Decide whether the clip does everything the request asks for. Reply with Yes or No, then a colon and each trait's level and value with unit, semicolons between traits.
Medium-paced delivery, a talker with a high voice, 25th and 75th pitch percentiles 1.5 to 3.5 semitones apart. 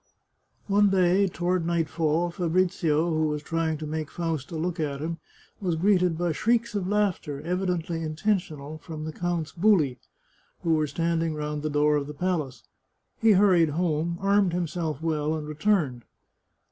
No: average, 160 wpm; medium, 165 Hz; average, 2.9 semitones